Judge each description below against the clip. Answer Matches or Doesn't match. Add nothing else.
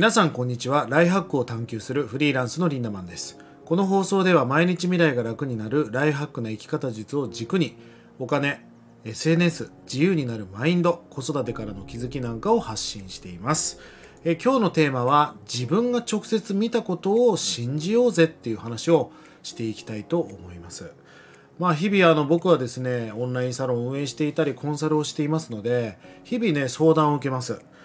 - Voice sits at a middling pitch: Matches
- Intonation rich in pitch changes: Matches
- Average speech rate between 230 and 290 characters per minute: Doesn't match